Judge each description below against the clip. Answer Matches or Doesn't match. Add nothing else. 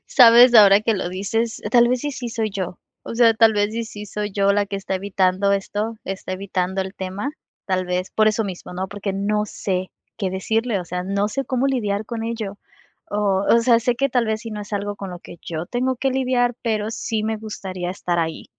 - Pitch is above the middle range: Matches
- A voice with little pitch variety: Doesn't match